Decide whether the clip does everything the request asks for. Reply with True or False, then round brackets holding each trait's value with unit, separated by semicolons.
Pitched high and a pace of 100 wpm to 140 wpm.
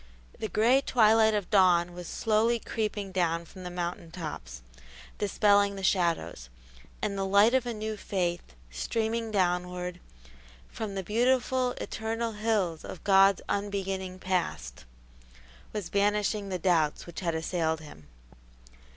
True (195 Hz; 135 wpm)